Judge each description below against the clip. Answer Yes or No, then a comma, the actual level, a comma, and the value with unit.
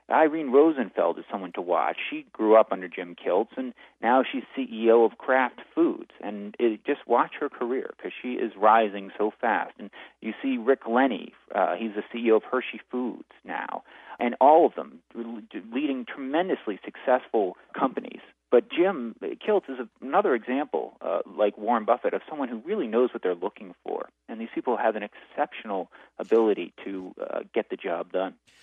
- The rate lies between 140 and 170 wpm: No, average, 180 wpm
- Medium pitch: No, low, 125 Hz